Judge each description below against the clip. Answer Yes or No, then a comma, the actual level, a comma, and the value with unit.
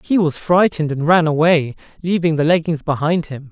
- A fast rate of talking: No, average, 190 wpm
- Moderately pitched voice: Yes, medium, 160 Hz